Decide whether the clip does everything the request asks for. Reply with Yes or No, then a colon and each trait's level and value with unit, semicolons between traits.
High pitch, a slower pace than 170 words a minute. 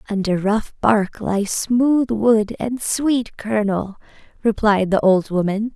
Yes: high, 215 Hz; slow, 135 wpm